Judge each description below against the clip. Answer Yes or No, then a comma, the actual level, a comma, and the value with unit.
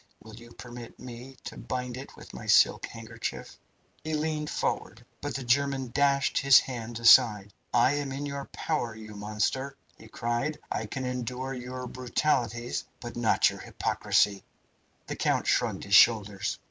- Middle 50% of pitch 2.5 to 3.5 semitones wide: Yes, average, 3.0 semitones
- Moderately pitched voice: No, low, 125 Hz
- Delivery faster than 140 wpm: Yes, average, 160 wpm